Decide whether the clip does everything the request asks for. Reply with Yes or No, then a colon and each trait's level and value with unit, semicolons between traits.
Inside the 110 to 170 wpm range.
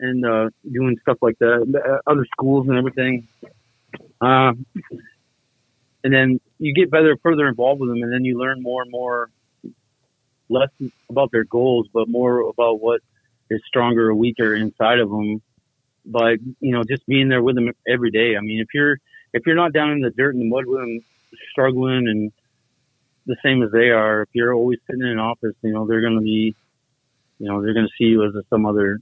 No: fast, 205 wpm